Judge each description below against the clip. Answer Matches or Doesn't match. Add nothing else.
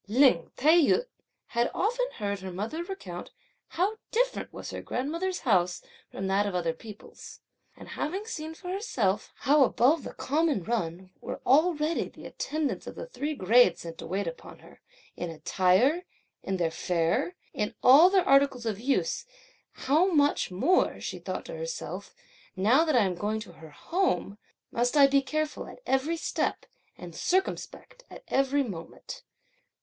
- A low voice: Doesn't match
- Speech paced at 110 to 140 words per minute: Doesn't match